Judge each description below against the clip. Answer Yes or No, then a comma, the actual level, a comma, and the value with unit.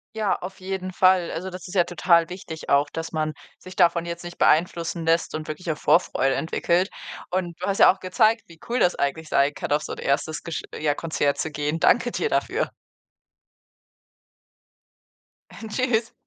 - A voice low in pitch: No, medium, 170 Hz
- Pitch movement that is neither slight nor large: Yes, average, 3.0 semitones